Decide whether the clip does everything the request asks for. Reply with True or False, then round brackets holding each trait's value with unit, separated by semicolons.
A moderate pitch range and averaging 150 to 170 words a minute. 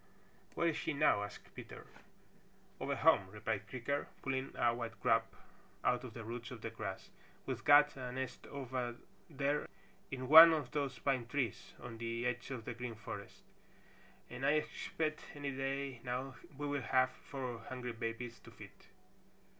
True (3.2 semitones; 165 wpm)